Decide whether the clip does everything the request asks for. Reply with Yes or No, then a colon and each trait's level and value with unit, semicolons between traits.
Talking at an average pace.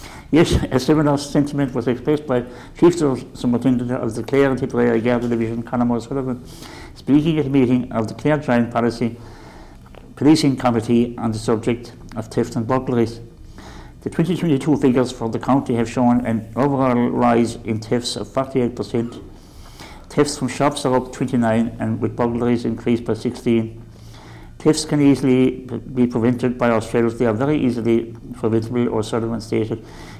Yes: average, 155 wpm